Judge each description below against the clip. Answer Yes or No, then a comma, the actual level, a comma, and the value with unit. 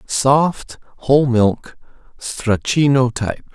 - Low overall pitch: Yes, low, 130 Hz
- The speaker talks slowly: Yes, slow, 85 wpm